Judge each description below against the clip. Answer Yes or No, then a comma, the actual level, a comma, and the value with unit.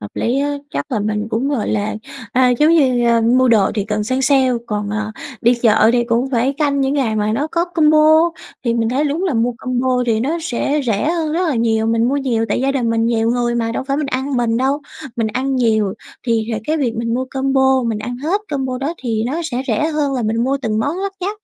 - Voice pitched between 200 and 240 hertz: No, very high, 250 Hz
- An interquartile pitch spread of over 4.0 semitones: No, average, 3.7 semitones